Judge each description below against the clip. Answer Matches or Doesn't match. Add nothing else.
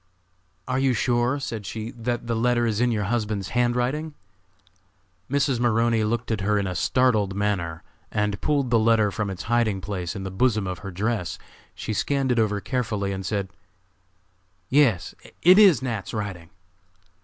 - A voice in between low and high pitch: Doesn't match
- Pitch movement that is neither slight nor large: Matches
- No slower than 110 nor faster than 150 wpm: Doesn't match